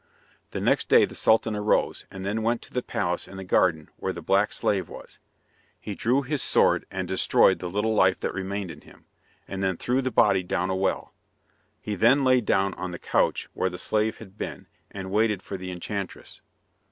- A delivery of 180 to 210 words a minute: Yes, fast, 205 wpm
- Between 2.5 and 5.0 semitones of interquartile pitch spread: Yes, average, 2.9 semitones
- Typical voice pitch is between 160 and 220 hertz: No, very low, 95 Hz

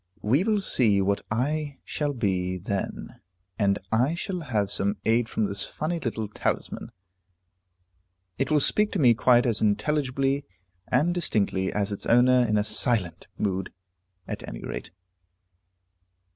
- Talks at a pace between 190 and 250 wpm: No, average, 145 wpm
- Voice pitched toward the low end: Yes, low, 120 Hz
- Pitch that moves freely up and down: Yes, wide, 6.1 semitones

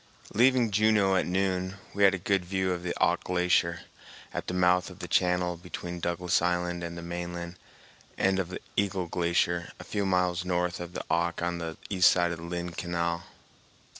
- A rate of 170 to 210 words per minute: Yes, average, 185 wpm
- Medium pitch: No, very low, 90 Hz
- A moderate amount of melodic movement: No, narrow, 1.3 semitones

